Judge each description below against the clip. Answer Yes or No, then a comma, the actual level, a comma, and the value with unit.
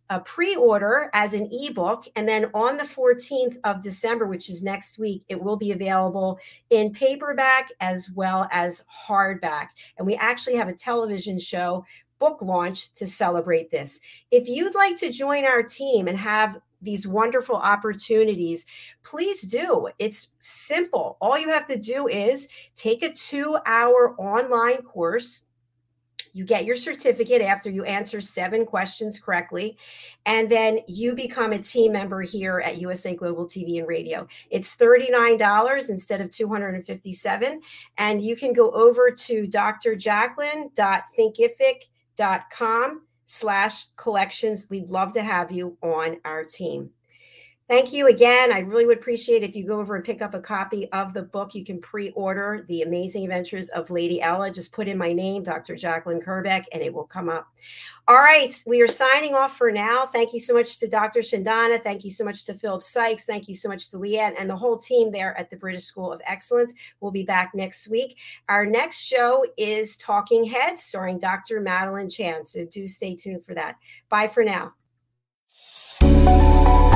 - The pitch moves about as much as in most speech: Yes, average, 4.4 semitones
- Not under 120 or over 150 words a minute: No, average, 170 wpm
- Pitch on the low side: No, high, 215 Hz